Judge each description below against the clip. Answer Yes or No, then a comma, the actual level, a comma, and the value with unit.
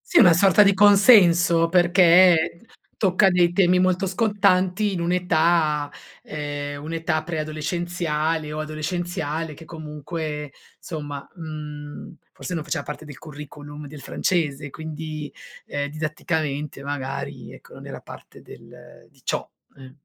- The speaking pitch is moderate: Yes, medium, 160 Hz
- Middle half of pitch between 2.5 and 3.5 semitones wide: Yes, average, 2.9 semitones